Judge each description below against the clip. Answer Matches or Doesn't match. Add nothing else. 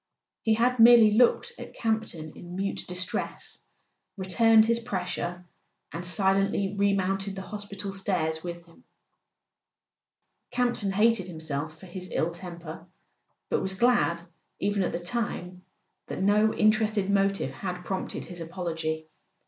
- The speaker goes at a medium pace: Doesn't match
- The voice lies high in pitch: Matches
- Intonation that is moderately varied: Matches